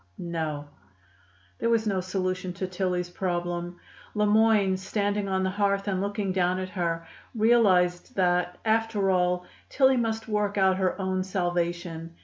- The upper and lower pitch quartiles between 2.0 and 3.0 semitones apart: Yes, narrow, 2.4 semitones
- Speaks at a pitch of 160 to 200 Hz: Yes, medium, 185 Hz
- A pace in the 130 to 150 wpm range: Yes, average, 145 wpm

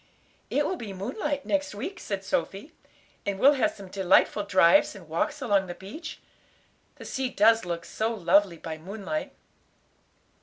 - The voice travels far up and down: Yes, wide, 6.0 semitones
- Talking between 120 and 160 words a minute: Yes, average, 155 wpm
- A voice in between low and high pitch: No, high, 205 Hz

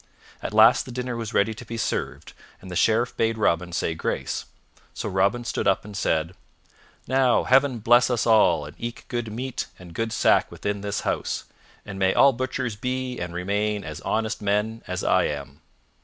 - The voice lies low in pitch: Yes, low, 110 Hz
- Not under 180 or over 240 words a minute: Yes, average, 185 wpm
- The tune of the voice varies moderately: Yes, average, 4.1 semitones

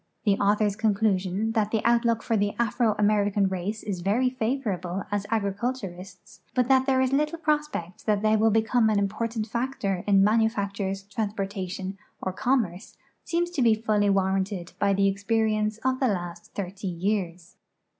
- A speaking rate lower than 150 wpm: No, average, 165 wpm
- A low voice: No, high, 210 Hz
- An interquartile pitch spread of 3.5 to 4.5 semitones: No, average, 2.8 semitones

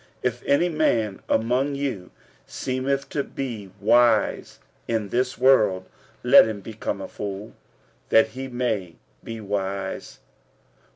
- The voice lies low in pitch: Yes, low, 115 Hz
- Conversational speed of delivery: No, slow, 120 wpm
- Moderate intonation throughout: Yes, average, 4.2 semitones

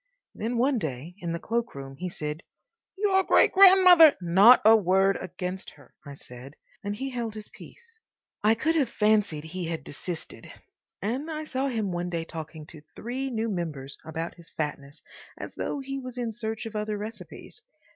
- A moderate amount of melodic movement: No, wide, 7.2 semitones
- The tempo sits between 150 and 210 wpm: Yes, average, 175 wpm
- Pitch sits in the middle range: No, high, 210 Hz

